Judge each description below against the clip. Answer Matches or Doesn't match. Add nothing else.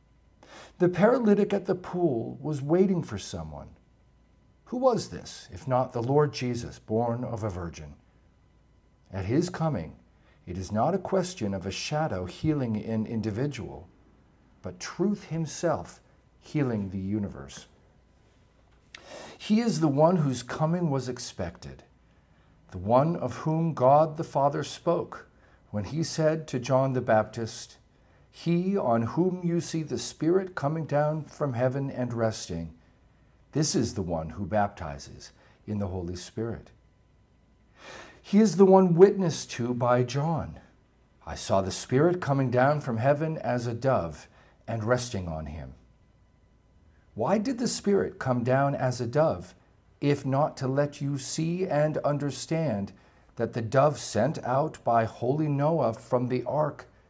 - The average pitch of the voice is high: Doesn't match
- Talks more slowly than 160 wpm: Matches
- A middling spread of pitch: Doesn't match